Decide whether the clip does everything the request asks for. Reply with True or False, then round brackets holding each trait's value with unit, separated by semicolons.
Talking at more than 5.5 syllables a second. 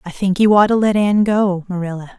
True (6.0 syllables/s)